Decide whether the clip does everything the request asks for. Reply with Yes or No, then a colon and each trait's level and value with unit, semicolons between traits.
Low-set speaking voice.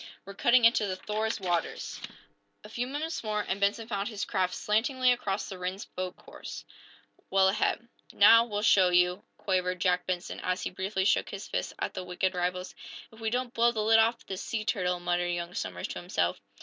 No: high, 195 Hz